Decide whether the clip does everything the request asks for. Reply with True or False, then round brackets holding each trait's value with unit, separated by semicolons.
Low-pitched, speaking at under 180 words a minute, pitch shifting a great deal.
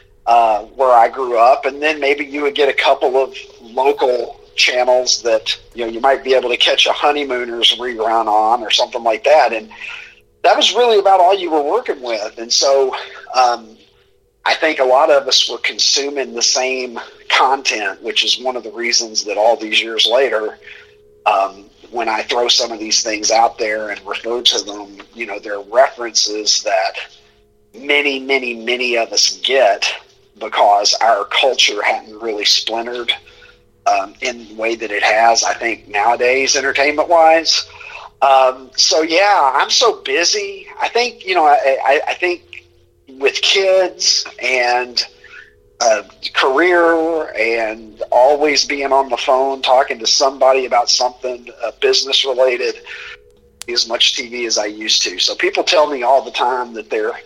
True (130 Hz; 170 wpm; 6.1 semitones)